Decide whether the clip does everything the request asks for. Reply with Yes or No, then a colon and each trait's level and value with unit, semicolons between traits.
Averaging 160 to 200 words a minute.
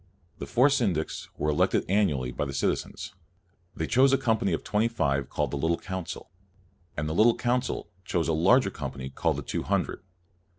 Yes: average, 180 wpm